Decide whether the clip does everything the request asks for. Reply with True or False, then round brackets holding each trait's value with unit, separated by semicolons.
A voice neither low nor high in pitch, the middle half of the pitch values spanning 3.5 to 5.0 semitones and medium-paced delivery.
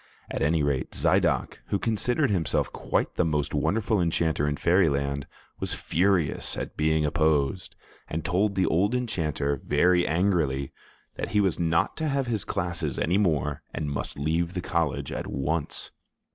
False (85 Hz; 4.6 semitones; 160 wpm)